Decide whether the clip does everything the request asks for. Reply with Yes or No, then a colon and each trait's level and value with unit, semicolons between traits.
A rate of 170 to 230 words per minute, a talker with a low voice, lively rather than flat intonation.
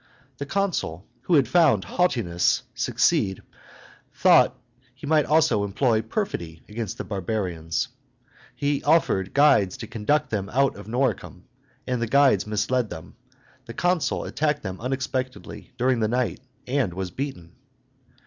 No: slow, 135 wpm; low, 120 Hz; wide, 6.3 semitones